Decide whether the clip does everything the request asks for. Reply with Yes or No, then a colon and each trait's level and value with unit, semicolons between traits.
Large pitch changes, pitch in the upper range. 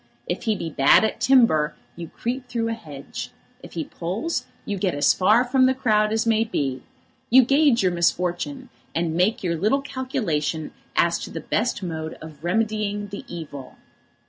Yes: wide, 6.2 semitones; high, 205 Hz